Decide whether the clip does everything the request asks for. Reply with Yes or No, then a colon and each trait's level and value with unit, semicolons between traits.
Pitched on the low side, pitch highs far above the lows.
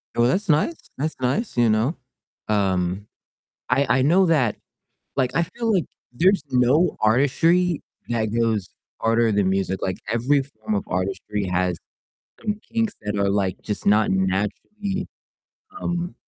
Yes: low, 120 Hz; wide, 8.4 semitones